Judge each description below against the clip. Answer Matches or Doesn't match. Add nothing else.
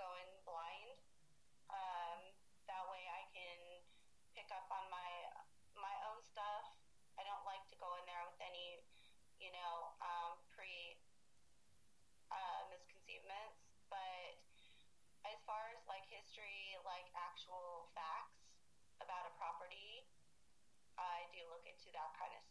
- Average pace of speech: Doesn't match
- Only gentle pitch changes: Matches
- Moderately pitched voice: Matches